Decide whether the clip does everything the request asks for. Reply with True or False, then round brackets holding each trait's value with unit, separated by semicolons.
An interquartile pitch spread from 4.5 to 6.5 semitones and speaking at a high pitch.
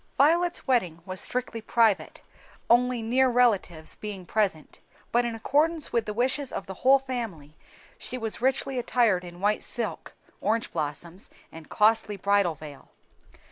True (5.2 semitones; 225 Hz)